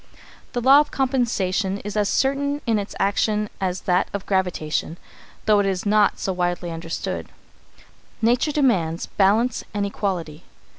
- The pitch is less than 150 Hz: No, high, 200 Hz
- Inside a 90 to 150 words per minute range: Yes, average, 145 wpm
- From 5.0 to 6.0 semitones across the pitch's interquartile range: No, average, 4.5 semitones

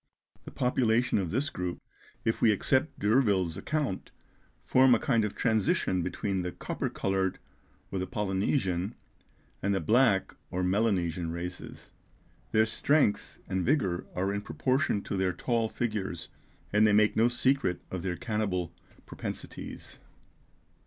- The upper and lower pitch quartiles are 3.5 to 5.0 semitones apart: Yes, average, 4.2 semitones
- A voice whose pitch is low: Yes, low, 100 Hz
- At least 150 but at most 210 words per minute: No, average, 140 wpm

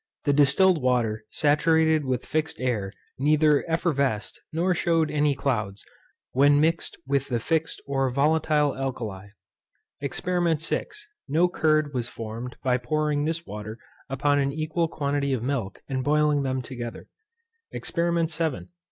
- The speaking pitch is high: No, medium, 145 Hz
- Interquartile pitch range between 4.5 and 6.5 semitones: No, average, 3.7 semitones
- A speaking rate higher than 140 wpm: No, slow, 135 wpm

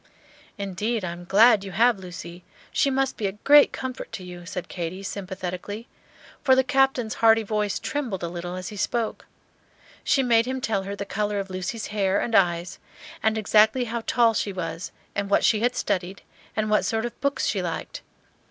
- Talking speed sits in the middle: Yes, average, 190 wpm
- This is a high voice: Yes, high, 210 Hz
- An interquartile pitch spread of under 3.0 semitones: No, average, 4.0 semitones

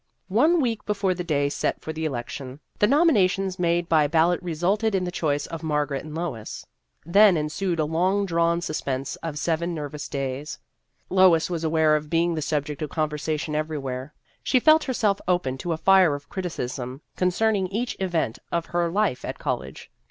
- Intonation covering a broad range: No, average, 3.9 semitones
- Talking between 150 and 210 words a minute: Yes, average, 180 wpm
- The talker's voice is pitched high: No, medium, 165 Hz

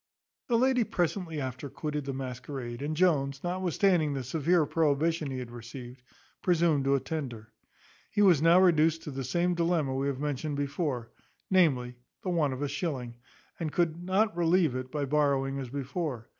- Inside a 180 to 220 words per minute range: No, average, 170 wpm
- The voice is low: No, medium, 150 Hz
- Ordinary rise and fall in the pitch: Yes, average, 4.2 semitones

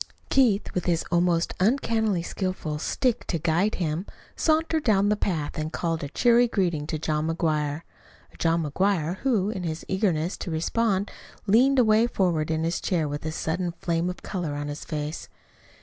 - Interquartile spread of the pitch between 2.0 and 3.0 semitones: No, average, 4.7 semitones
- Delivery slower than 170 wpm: No, average, 175 wpm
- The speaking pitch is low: No, medium, 175 Hz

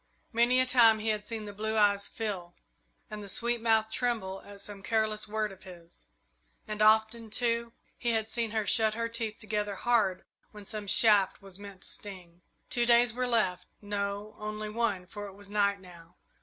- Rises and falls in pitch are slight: Yes, narrow, 2.1 semitones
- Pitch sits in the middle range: No, high, 215 Hz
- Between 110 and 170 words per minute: No, average, 190 wpm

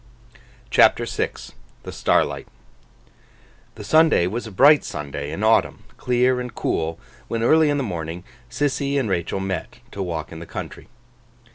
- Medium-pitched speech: No, low, 110 Hz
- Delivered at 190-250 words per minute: No, average, 150 wpm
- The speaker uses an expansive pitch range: Yes, wide, 7.9 semitones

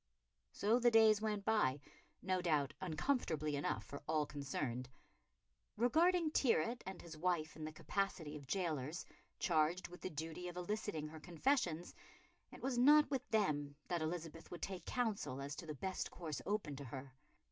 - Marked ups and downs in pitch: Yes, wide, 5.7 semitones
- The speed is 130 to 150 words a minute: No, average, 165 wpm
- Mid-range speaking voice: Yes, medium, 175 Hz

